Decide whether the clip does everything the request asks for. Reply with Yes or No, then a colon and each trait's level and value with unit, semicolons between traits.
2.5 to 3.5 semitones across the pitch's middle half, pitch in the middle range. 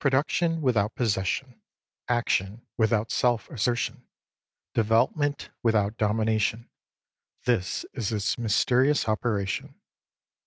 No: average, 2.8 semitones; low, 115 Hz